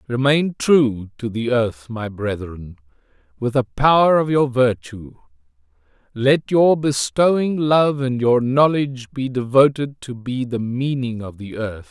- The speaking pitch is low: Yes, low, 125 Hz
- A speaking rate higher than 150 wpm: No, average, 145 wpm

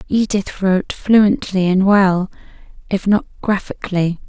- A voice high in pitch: Yes, high, 195 Hz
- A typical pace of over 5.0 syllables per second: No, 4.2 syllables/s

